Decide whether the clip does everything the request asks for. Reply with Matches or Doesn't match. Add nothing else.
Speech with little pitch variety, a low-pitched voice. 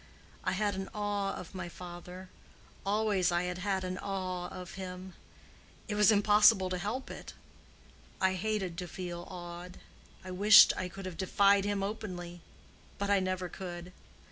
Doesn't match